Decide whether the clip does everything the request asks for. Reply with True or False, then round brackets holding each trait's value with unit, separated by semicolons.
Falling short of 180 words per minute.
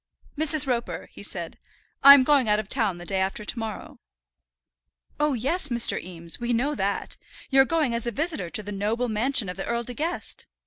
False (195 wpm)